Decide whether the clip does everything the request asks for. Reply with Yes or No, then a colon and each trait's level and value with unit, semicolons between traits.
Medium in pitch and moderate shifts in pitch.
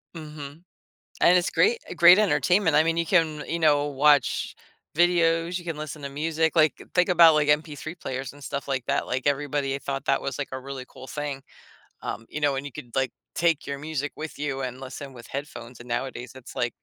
Yes: medium, 145 Hz; average, 3.2 semitones